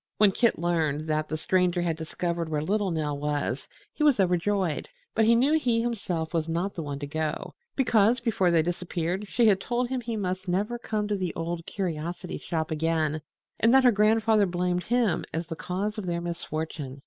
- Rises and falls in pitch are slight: No, average, 4.8 semitones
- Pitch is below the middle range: No, medium, 180 Hz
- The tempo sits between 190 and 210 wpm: Yes, average, 195 wpm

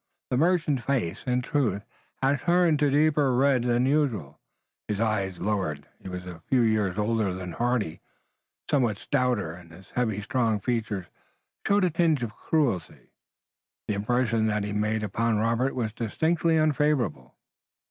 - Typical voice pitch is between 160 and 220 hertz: No, low, 115 Hz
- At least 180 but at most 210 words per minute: No, average, 155 wpm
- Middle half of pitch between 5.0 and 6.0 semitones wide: Yes, average, 5.3 semitones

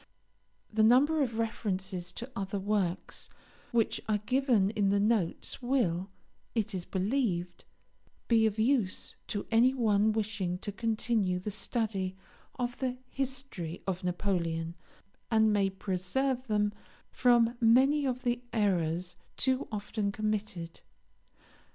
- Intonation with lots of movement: No, average, 4.1 semitones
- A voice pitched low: No, high, 215 Hz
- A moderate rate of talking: No, slow, 125 wpm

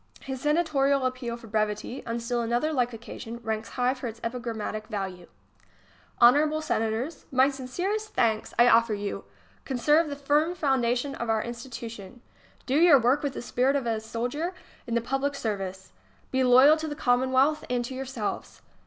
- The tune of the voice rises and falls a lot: No, average, 3.4 semitones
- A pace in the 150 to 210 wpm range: Yes, average, 170 wpm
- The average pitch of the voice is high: Yes, very high, 250 Hz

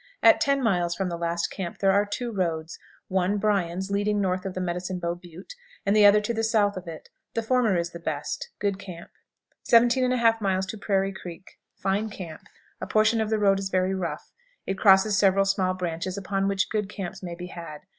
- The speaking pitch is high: Yes, high, 195 Hz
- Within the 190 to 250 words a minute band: Yes, fast, 205 wpm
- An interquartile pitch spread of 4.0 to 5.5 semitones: No, average, 2.7 semitones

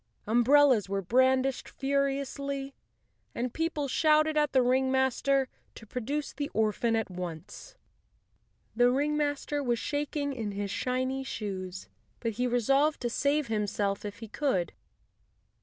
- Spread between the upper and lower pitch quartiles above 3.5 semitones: Yes, average, 4.2 semitones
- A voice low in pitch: No, very high, 260 Hz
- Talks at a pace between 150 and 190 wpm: No, slow, 135 wpm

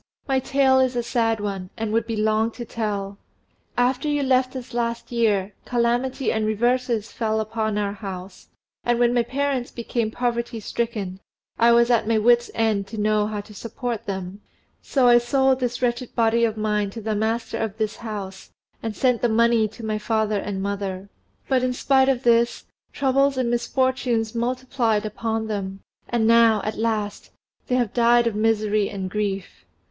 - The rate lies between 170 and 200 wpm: Yes, average, 180 wpm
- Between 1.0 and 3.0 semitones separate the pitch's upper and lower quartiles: Yes, narrow, 2.4 semitones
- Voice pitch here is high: Yes, high, 230 Hz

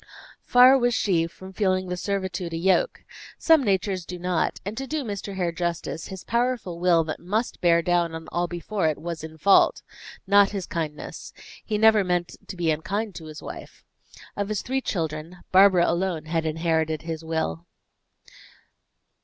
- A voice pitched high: No, medium, 180 Hz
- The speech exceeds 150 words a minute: Yes, average, 170 wpm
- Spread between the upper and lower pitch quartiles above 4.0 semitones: No, average, 3.5 semitones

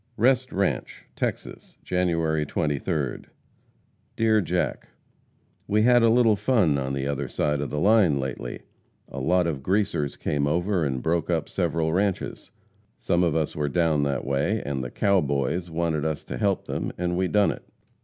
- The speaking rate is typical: Yes, average, 170 wpm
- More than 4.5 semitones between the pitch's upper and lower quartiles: Yes, wide, 5.4 semitones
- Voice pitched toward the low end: Yes, very low, 85 Hz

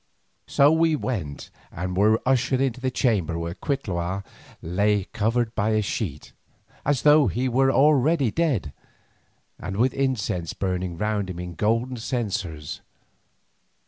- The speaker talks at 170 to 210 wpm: No, slow, 135 wpm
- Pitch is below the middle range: Yes, low, 110 Hz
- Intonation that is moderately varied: No, wide, 6.2 semitones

